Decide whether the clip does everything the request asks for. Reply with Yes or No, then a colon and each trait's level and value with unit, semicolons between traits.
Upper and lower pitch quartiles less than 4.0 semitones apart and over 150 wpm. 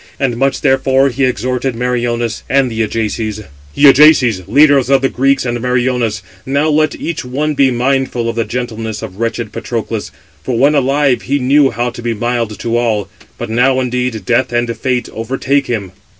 Yes: average, 2.7 semitones; average, 180 wpm